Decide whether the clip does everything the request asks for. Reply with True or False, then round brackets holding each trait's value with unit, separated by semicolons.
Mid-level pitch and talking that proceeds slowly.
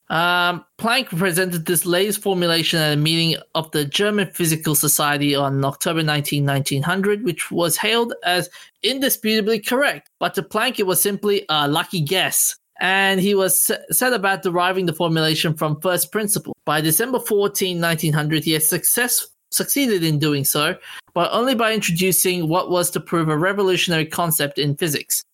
False (175 Hz; 160 wpm)